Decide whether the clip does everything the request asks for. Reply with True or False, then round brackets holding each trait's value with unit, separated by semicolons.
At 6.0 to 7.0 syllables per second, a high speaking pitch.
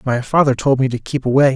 False (6.3 syllables/s; 135 Hz)